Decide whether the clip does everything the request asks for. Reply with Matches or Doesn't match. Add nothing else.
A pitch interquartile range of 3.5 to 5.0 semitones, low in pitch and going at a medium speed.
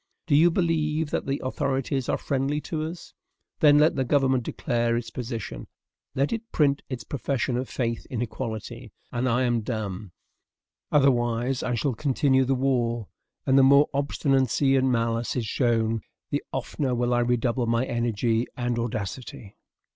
Doesn't match